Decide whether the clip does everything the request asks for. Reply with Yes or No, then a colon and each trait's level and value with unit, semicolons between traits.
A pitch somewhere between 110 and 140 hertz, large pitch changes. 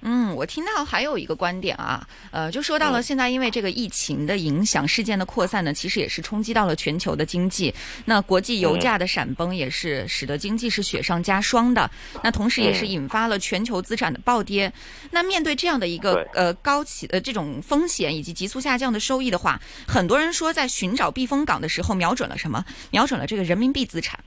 No: high, 210 Hz; wide, 5.9 semitones